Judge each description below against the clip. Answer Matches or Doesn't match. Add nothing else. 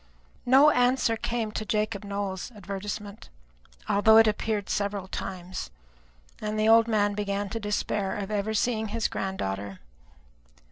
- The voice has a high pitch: Matches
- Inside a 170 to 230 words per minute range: Doesn't match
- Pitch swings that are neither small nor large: Doesn't match